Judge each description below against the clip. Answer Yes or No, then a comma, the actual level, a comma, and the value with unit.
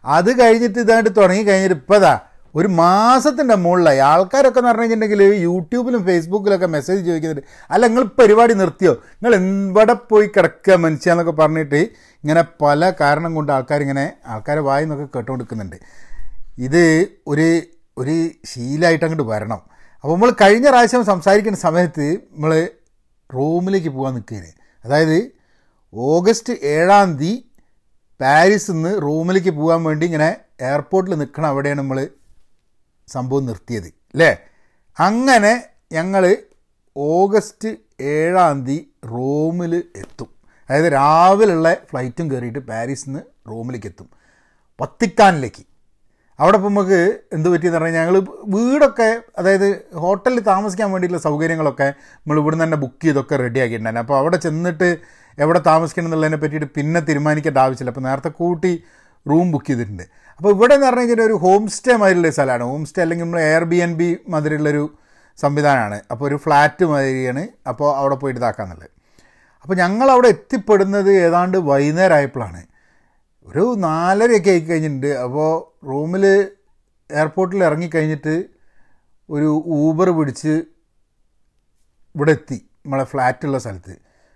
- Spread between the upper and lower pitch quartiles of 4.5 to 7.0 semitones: Yes, wide, 5.5 semitones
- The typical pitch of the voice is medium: Yes, medium, 160 Hz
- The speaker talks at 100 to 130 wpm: Yes, average, 120 wpm